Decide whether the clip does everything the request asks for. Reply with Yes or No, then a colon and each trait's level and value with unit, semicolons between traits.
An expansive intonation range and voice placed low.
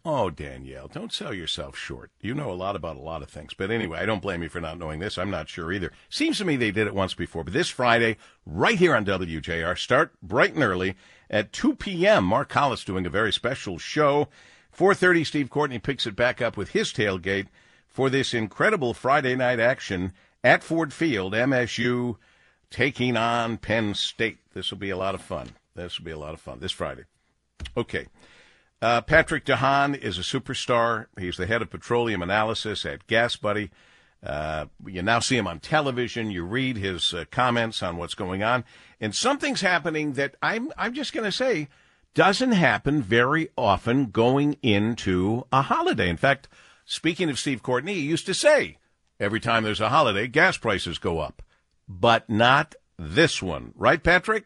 Yes: wide, 6.7 semitones; low, 115 Hz